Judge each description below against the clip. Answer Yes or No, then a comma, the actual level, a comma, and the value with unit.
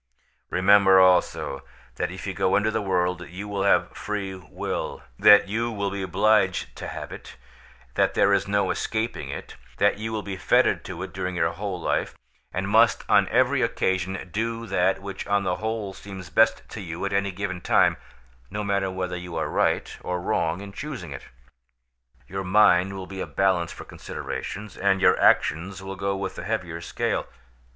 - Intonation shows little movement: Yes, narrow, 2.1 semitones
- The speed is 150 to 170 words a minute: No, average, 185 wpm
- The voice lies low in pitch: Yes, very low, 95 Hz